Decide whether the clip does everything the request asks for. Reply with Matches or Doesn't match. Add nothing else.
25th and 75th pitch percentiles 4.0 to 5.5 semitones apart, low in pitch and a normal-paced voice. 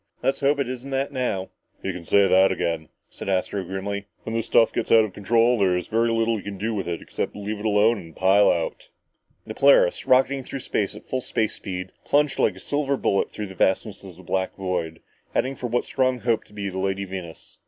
Doesn't match